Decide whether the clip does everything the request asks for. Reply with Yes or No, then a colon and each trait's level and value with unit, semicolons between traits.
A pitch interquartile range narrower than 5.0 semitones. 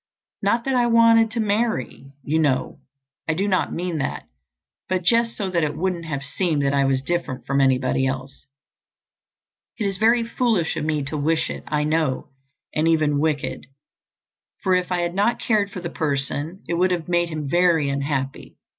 No: average, 5.3 semitones